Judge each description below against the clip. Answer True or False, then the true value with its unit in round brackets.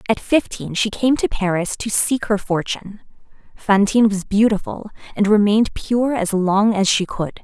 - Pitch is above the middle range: True (205 Hz)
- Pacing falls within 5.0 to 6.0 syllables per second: False (4.8 syllables/s)